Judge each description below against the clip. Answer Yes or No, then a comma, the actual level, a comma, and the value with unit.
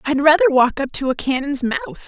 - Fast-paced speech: Yes, fast, 230 wpm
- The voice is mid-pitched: No, very high, 260 Hz